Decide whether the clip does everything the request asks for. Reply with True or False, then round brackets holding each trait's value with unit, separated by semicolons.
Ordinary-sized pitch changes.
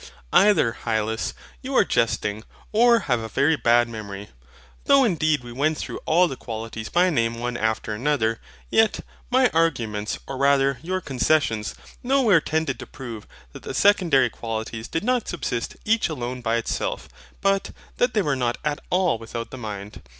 False (7.4 semitones)